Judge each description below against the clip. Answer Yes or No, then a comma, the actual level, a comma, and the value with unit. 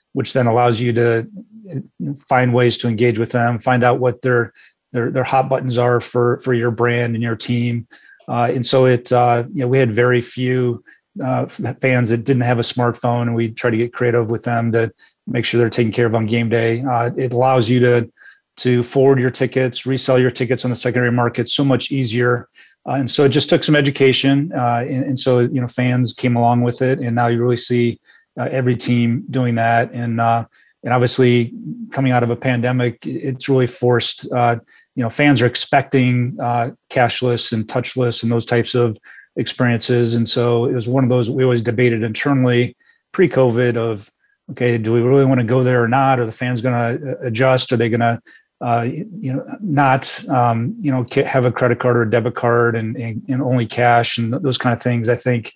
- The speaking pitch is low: Yes, low, 125 Hz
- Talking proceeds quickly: Yes, fast, 215 wpm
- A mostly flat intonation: Yes, narrow, 1.6 semitones